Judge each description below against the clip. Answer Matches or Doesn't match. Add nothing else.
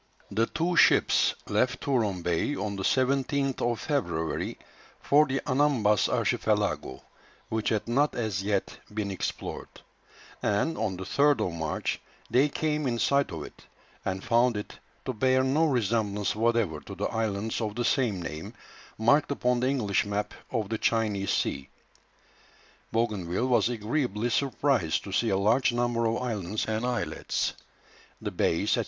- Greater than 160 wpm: Doesn't match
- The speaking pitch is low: Matches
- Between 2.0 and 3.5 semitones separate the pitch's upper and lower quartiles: Doesn't match